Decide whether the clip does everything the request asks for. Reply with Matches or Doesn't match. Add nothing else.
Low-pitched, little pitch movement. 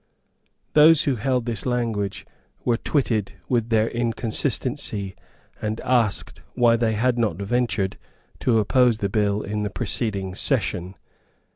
Doesn't match